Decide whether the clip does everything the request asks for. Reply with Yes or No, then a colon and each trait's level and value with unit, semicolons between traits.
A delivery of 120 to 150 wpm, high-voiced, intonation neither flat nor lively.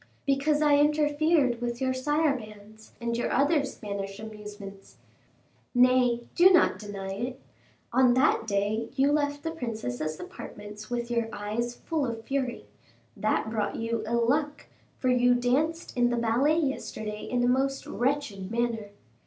Yes: average, 145 wpm; high, 245 Hz; average, 4.3 semitones